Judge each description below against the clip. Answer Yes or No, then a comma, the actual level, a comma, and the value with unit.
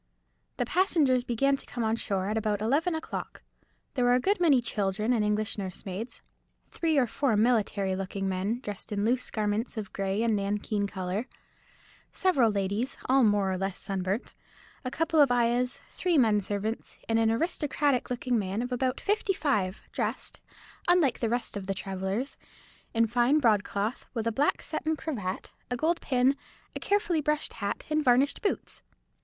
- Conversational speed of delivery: Yes, average, 170 wpm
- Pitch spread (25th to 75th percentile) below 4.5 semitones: No, average, 5.0 semitones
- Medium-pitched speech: No, high, 230 Hz